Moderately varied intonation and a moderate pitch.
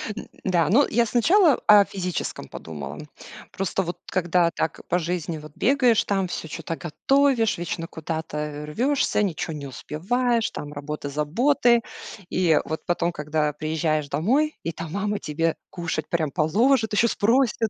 No: wide, 6.6 semitones; medium, 175 Hz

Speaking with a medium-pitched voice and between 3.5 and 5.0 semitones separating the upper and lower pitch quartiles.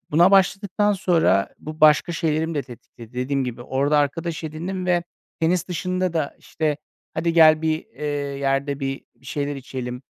Yes: medium, 155 Hz; average, 3.9 semitones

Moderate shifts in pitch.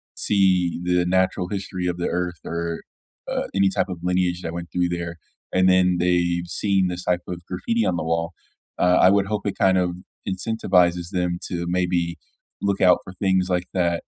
No: narrow, 1.1 semitones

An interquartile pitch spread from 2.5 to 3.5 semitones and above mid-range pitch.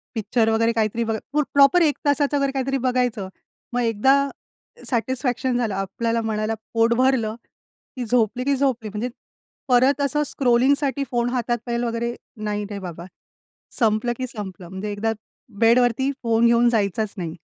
Yes: average, 3.0 semitones; high, 235 Hz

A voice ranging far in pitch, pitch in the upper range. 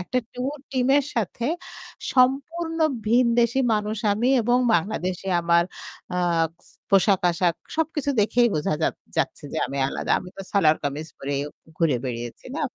Yes: wide, 6.8 semitones; high, 210 Hz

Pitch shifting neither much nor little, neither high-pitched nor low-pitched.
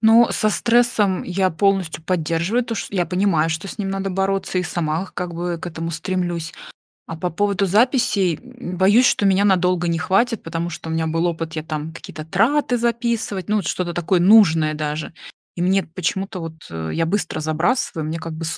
Yes: average, 3.6 semitones; medium, 180 Hz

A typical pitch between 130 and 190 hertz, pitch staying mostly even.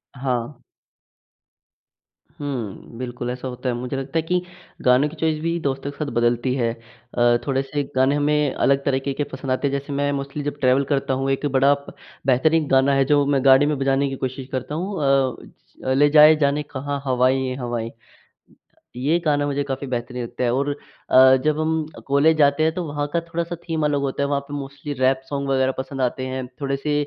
Yes: low, 135 Hz; narrow, 2.0 semitones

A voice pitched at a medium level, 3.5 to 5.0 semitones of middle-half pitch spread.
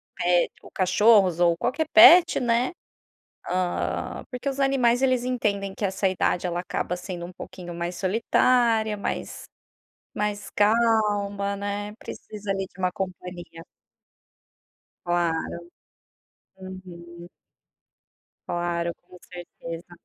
No: high, 195 Hz; average, 3.9 semitones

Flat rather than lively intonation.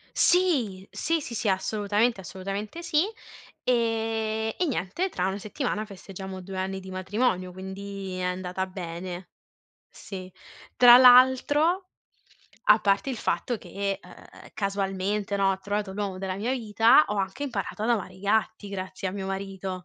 No: average, 3.1 semitones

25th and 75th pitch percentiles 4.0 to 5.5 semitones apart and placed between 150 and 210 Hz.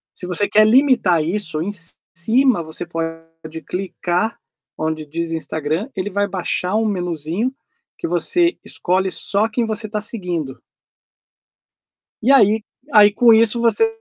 Yes: average, 5.0 semitones; high, 190 Hz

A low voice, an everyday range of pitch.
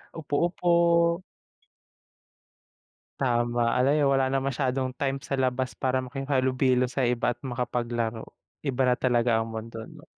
No: low, 130 Hz; narrow, 2.2 semitones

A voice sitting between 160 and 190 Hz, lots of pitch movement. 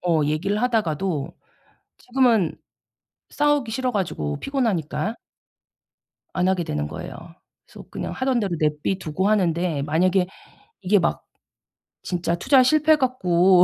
Yes: medium, 185 Hz; wide, 6.4 semitones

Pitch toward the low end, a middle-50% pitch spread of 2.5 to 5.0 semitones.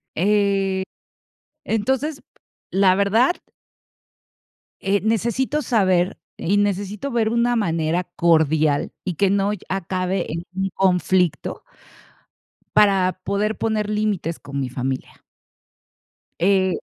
No: high, 195 Hz; average, 2.8 semitones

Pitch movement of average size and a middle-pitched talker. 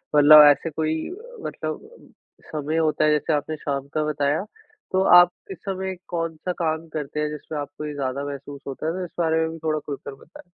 No: narrow, 2.2 semitones; medium, 155 Hz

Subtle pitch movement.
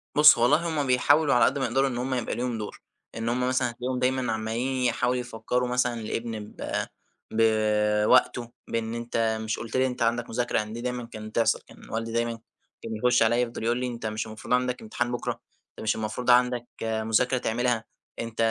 Yes: narrow, 1.9 semitones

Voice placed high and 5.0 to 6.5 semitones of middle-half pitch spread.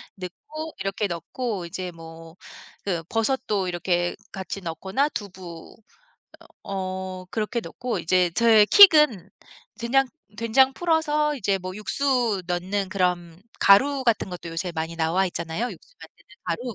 Yes: high, 195 Hz; wide, 5.5 semitones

